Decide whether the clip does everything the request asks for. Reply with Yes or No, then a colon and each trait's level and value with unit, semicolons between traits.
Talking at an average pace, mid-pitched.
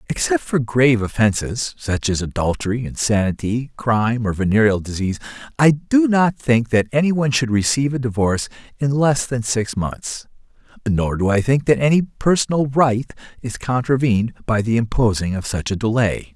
No: average, 160 wpm; low, 120 Hz